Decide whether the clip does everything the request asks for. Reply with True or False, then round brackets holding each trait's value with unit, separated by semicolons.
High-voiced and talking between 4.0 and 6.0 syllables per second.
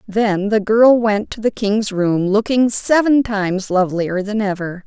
True (210 Hz; 4.3 syllables/s)